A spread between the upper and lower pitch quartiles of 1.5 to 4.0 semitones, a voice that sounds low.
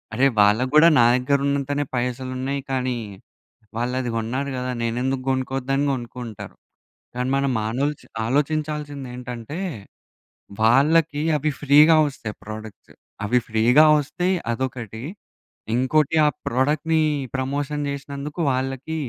Yes: average, 2.7 semitones; low, 130 Hz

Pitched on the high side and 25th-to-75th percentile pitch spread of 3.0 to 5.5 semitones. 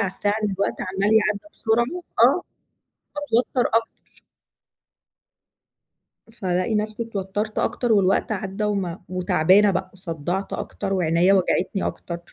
No: high, 195 Hz; narrow, 2.6 semitones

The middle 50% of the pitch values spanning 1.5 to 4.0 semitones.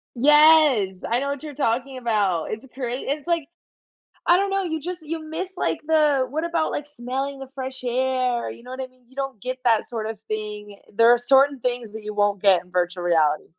No: average, 5.2 semitones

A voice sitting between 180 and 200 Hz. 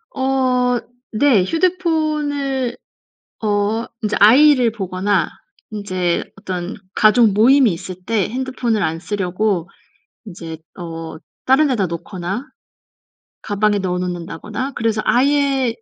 No: high, 215 Hz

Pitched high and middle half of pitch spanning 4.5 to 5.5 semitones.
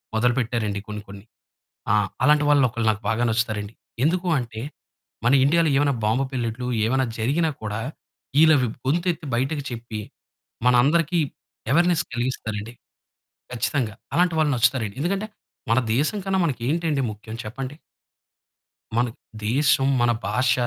No: low, 130 Hz; average, 5.0 semitones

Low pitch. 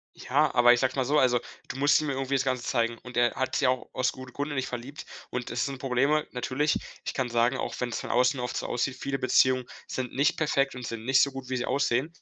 Yes: low, 130 Hz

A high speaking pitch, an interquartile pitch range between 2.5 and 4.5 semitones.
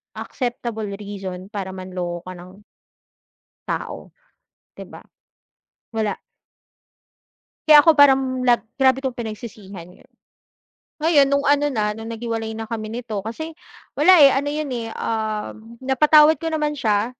No: high, 230 Hz; average, 5.0 semitones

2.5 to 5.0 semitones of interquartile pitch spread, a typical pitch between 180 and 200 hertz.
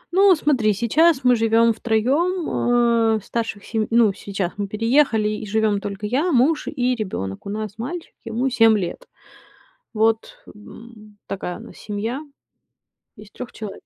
No: average, 2.9 semitones; high, 225 Hz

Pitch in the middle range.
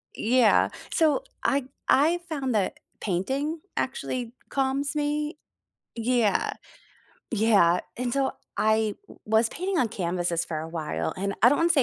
No: high, 245 Hz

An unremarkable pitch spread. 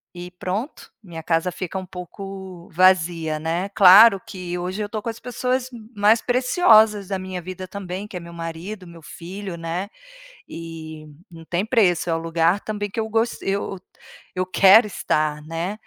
Yes: average, 3.3 semitones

